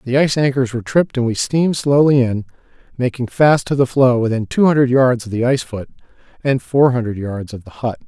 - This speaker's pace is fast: Yes, fast, 225 wpm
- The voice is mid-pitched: No, low, 125 Hz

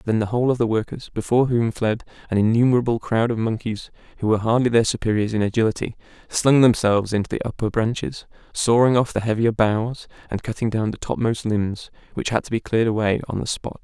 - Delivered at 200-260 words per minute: Yes, fast, 205 wpm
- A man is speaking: Yes, male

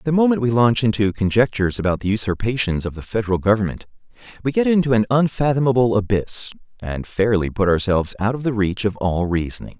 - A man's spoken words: Yes, male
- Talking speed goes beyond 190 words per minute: No, average, 185 wpm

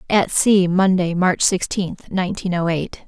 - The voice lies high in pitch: No, medium, 180 Hz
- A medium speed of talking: Yes, average, 155 wpm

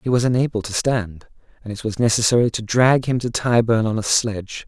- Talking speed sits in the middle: No, fast, 220 wpm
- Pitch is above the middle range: No, low, 115 Hz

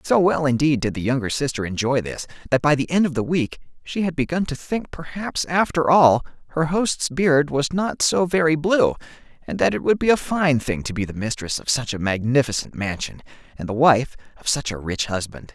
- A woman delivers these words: No, male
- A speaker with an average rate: No, fast, 220 wpm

